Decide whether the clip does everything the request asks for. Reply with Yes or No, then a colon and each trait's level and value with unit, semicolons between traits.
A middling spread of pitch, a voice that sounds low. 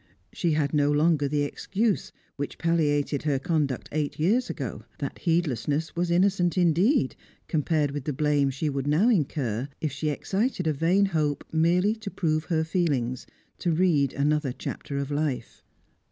No: average, 3.3 semitones; medium, 155 Hz